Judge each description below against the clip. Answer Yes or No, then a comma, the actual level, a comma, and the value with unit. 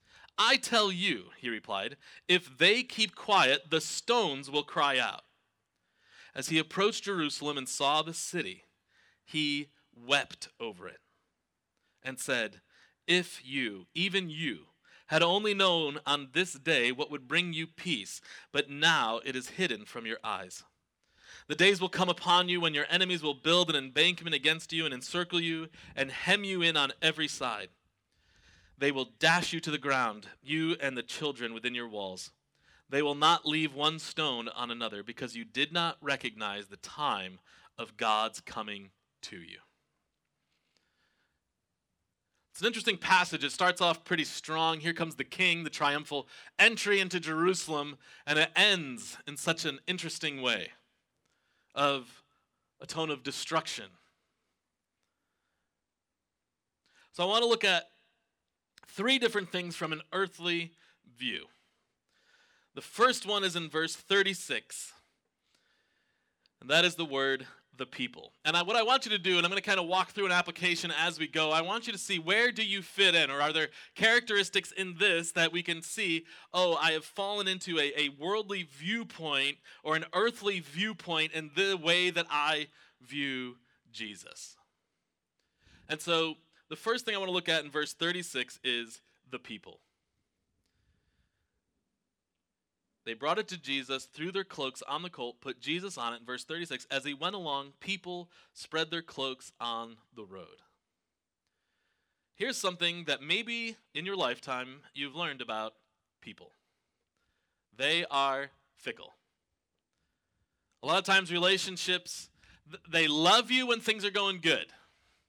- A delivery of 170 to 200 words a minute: No, average, 155 wpm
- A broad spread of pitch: No, average, 4.9 semitones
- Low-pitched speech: No, medium, 160 Hz